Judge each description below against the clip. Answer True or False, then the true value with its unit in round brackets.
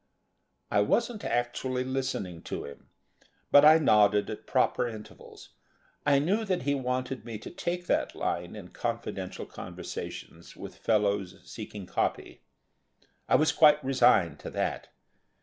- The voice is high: False (125 Hz)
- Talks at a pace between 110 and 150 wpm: True (135 wpm)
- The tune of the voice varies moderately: False (5.7 semitones)